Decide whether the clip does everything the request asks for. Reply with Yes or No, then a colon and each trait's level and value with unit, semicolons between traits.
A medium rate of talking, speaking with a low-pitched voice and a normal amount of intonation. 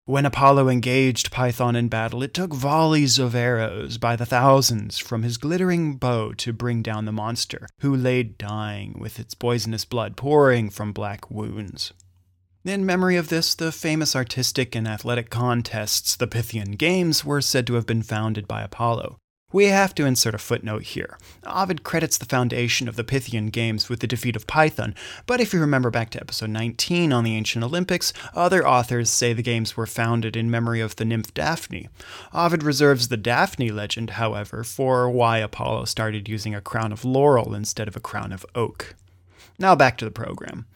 Yes: average, 185 wpm; low, 120 Hz; average, 3.7 semitones